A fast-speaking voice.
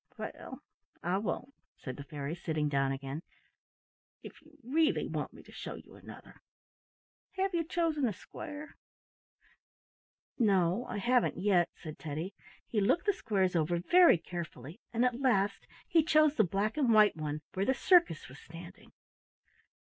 No: average, 155 wpm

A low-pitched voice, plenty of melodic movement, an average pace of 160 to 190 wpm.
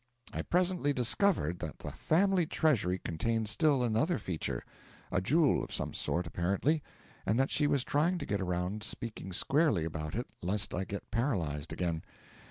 Yes: low, 110 Hz; wide, 9.0 semitones; average, 165 wpm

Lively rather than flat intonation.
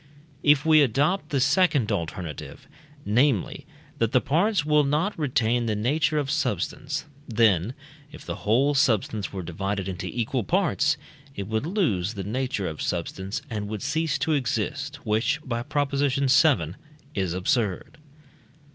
Yes: wide, 6.2 semitones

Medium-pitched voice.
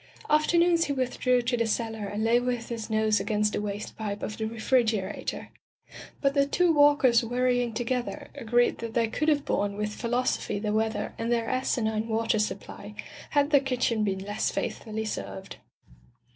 No: high, 230 Hz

